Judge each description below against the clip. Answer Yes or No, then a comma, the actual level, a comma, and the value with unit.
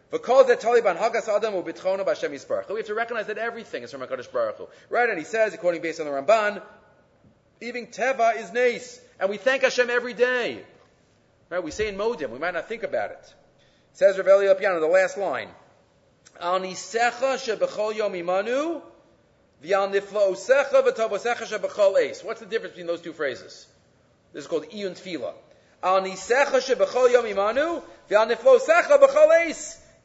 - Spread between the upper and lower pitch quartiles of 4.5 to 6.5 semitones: Yes, average, 5.1 semitones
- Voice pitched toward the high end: Yes, high, 225 Hz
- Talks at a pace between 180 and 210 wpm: Yes, average, 190 wpm